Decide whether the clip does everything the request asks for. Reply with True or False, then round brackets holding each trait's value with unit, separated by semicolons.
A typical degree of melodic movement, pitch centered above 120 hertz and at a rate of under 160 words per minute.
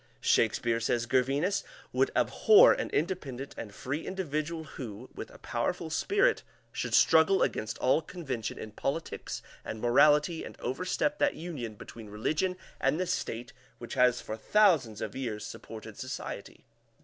False (6.5 semitones; 135 Hz; 145 wpm)